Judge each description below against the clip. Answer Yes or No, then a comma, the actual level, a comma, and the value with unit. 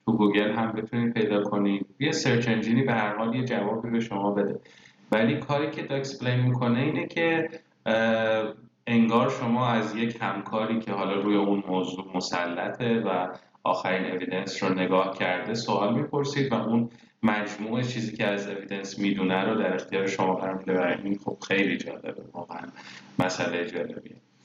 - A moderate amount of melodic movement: Yes, average, 3.2 semitones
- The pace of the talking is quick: Yes, fast, 160 wpm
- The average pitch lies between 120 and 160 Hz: No, low, 110 Hz